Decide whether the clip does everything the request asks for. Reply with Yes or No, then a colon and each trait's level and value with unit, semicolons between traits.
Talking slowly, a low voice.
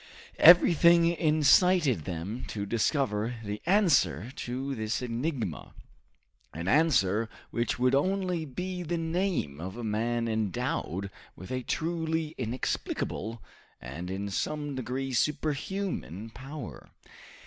Yes: slow, 110 wpm; low, 130 Hz